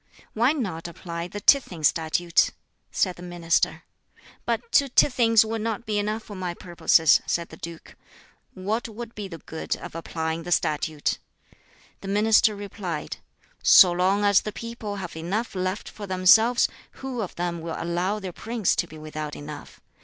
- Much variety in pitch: No, average, 4.5 semitones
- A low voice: No, medium, 185 Hz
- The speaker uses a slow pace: No, average, 165 wpm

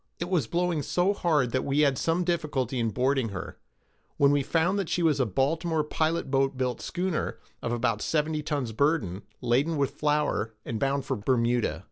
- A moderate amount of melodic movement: Yes, average, 4.4 semitones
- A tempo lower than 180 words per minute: No, average, 185 wpm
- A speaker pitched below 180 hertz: Yes, medium, 140 Hz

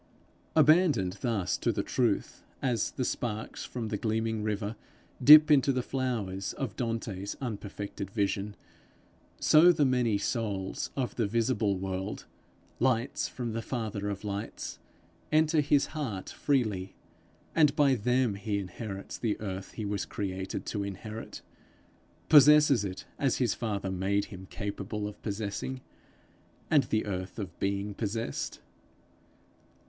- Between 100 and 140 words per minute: Yes, slow, 135 wpm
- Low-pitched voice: Yes, low, 110 Hz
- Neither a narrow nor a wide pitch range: Yes, average, 4.2 semitones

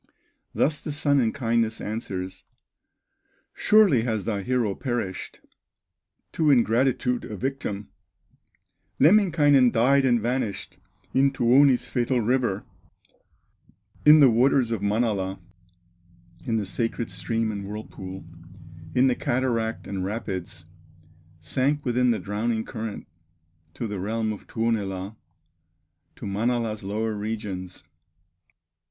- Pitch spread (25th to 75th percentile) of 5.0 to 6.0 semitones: No, average, 3.8 semitones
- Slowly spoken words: Yes, slow, 110 wpm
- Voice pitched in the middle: No, low, 115 Hz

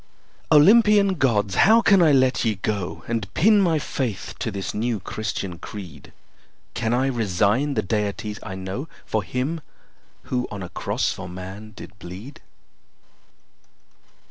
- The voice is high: No, low, 110 Hz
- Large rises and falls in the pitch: Yes, wide, 6.1 semitones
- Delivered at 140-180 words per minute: Yes, average, 145 wpm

